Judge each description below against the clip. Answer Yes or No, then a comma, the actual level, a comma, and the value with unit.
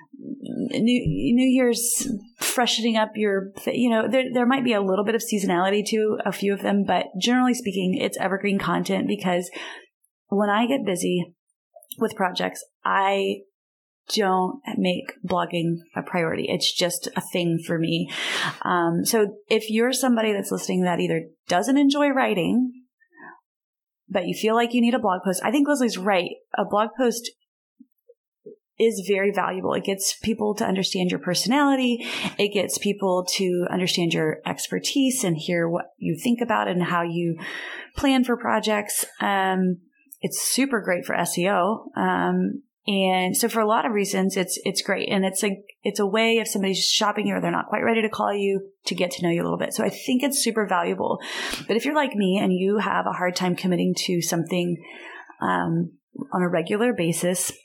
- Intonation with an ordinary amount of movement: Yes, average, 4.8 semitones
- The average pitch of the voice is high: Yes, high, 200 Hz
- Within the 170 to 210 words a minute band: Yes, average, 180 wpm